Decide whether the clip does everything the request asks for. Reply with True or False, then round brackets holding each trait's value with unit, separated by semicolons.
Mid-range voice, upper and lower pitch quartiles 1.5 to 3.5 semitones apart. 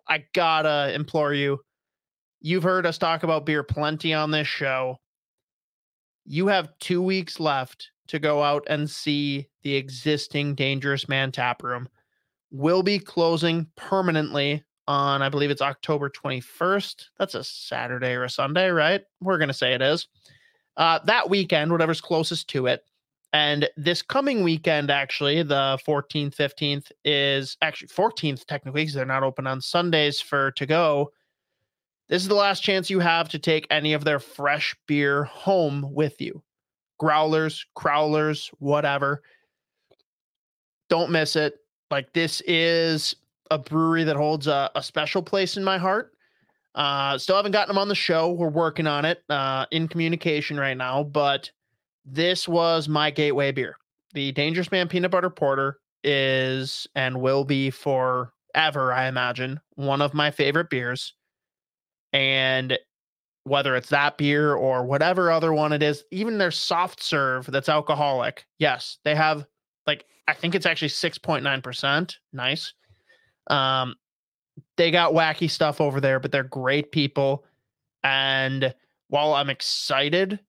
True (150 Hz; 3.0 semitones)